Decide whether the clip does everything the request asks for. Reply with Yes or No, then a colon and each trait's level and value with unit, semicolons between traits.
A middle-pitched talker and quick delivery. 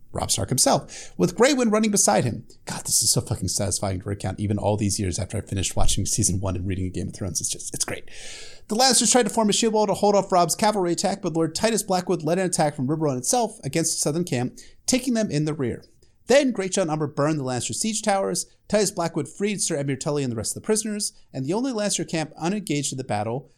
Yes: medium, 160 Hz; fast, 250 wpm